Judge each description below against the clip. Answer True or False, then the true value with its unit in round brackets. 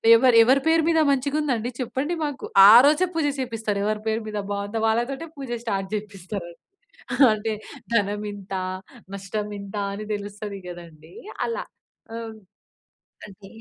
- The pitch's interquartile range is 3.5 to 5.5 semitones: True (4.5 semitones)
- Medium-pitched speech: False (220 Hz)